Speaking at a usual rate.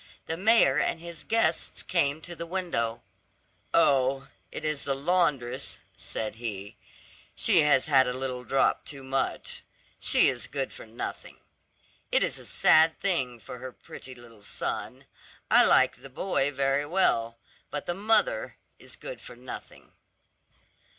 Yes: average, 150 wpm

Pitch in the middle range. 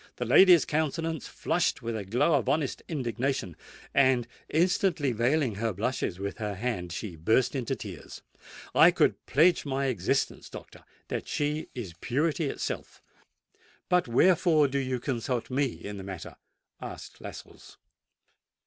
No: low, 130 Hz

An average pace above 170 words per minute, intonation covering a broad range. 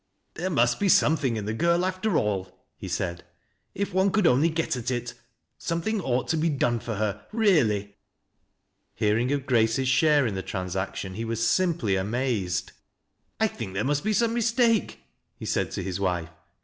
Yes: average, 185 wpm; wide, 8.6 semitones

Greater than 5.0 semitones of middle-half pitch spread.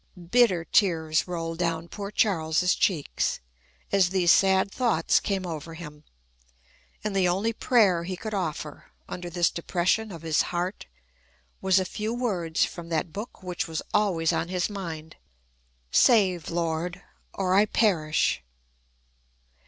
No: average, 3.2 semitones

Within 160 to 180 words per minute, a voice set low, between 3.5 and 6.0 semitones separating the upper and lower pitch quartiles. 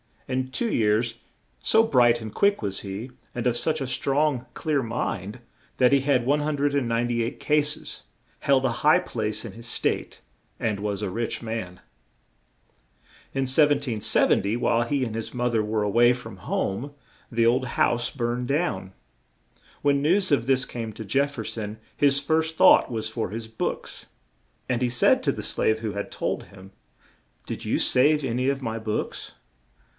Yes: average, 170 wpm; low, 120 Hz; average, 3.9 semitones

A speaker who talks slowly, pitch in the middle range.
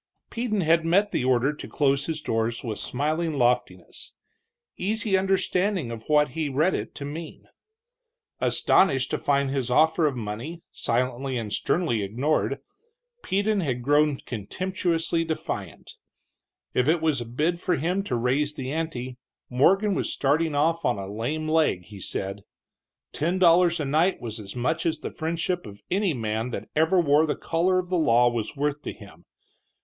No: average, 165 wpm; medium, 150 Hz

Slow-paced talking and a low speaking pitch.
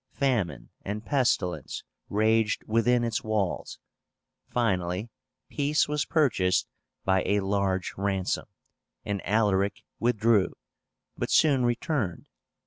Yes: slow, 100 wpm; low, 105 Hz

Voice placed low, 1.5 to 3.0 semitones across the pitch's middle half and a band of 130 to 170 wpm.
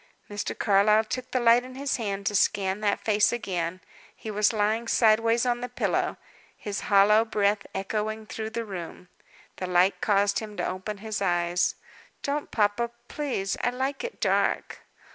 No: high, 215 Hz; average, 2.7 semitones; average, 165 wpm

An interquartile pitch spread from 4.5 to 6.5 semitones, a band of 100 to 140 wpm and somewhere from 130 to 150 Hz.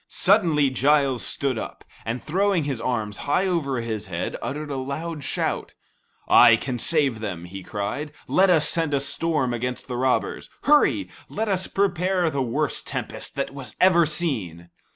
No: wide, 5.6 semitones; average, 165 wpm; medium, 140 Hz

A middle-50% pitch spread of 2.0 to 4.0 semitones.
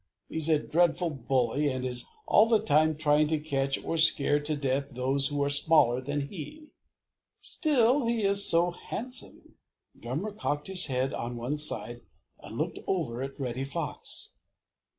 No: average, 4.6 semitones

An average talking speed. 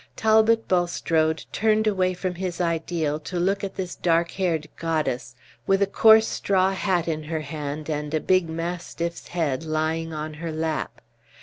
Yes: average, 165 wpm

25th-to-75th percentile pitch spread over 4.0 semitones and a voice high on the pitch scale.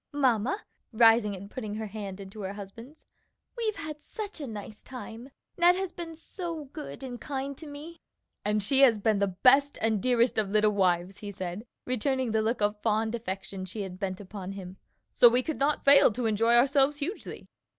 Yes: wide, 5.5 semitones; high, 230 Hz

